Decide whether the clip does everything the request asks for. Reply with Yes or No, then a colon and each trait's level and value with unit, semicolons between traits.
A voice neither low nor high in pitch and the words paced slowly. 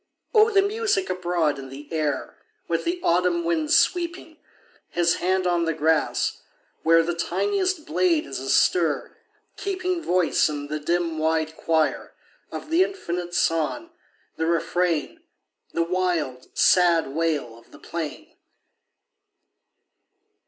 Yes: medium, 170 Hz; slow, 125 wpm